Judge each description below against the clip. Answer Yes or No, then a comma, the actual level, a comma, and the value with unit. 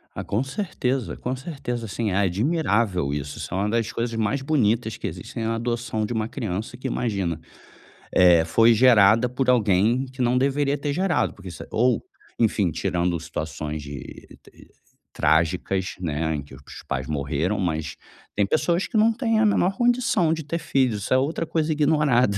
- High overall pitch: No, low, 115 Hz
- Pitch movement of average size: No, wide, 6.9 semitones